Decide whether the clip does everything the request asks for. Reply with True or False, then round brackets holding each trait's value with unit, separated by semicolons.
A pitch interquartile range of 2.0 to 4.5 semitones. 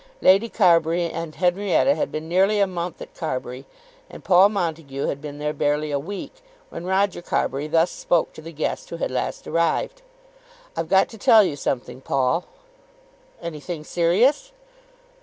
True (4.2 semitones)